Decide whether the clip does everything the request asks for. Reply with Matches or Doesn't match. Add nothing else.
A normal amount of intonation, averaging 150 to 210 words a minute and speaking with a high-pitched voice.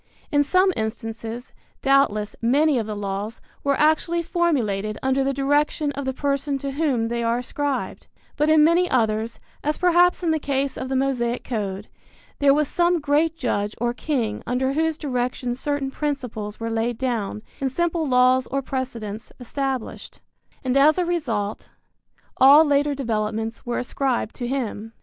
Matches